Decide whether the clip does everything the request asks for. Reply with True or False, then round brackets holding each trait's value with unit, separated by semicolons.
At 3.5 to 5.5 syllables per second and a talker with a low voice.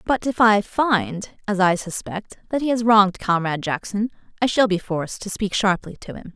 False (5.1 syllables/s; 200 Hz)